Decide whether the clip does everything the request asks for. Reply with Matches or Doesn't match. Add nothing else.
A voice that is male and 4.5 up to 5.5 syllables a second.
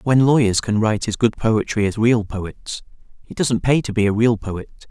Matches